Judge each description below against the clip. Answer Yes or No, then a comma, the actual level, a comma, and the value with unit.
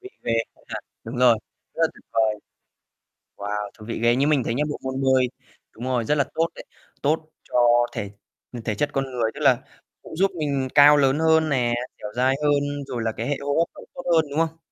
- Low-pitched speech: Yes, low, 130 Hz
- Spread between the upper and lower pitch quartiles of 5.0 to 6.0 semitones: No, average, 3.9 semitones